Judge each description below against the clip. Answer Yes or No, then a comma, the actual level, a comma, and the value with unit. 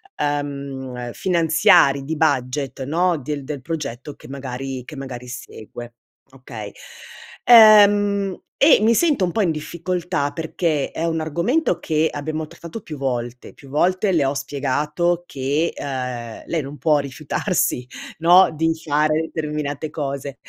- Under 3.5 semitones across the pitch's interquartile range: No, average, 3.8 semitones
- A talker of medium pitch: Yes, medium, 150 Hz